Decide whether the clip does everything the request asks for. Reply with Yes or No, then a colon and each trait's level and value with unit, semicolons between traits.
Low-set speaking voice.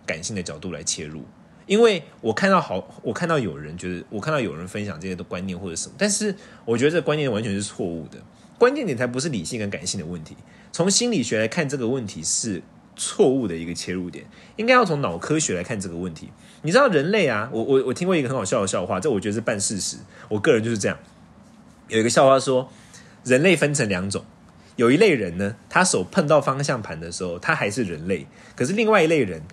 Yes: low, 115 Hz